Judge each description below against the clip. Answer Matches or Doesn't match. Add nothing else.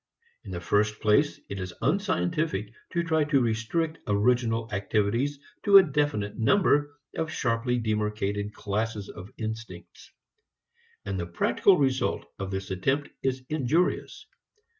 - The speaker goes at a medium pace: Doesn't match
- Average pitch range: Doesn't match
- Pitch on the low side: Matches